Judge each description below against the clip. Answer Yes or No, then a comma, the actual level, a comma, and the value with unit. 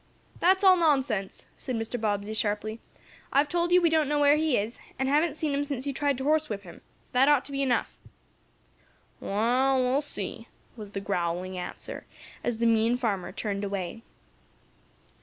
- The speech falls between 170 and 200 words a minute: Yes, average, 175 wpm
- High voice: Yes, very high, 250 Hz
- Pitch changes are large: Yes, wide, 5.7 semitones